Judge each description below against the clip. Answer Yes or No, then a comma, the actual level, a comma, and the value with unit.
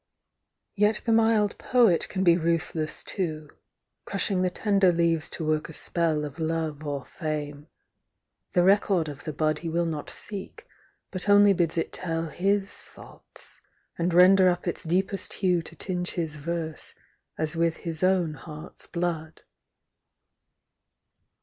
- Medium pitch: Yes, medium, 170 Hz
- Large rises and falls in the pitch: No, average, 3.2 semitones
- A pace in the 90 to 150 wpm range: Yes, average, 145 wpm